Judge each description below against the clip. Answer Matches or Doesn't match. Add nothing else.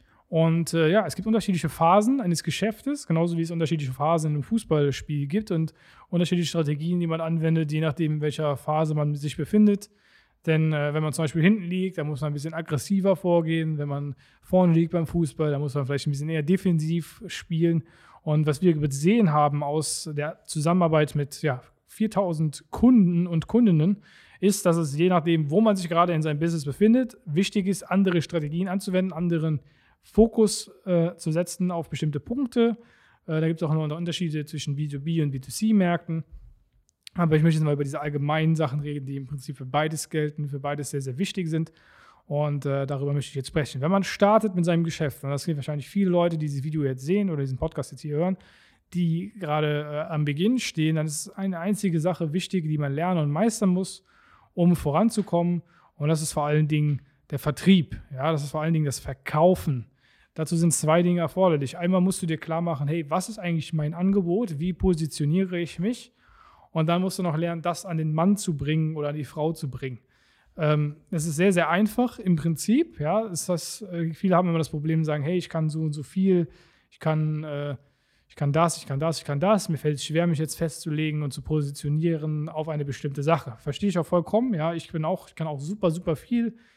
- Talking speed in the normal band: Doesn't match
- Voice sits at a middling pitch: Matches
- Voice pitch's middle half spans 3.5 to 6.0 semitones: Doesn't match